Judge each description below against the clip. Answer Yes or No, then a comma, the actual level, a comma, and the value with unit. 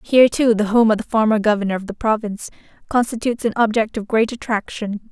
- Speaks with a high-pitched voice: Yes, high, 220 Hz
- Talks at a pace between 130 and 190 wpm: No, average, 200 wpm